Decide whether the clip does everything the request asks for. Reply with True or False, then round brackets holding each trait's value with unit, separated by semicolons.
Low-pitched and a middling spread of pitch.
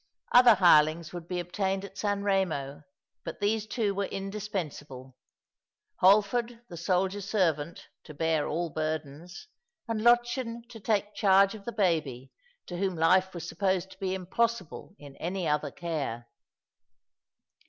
False (185 Hz; 4.2 semitones)